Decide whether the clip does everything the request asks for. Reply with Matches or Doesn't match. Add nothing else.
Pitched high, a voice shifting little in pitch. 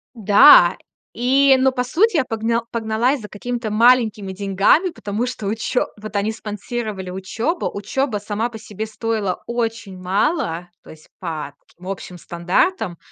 Doesn't match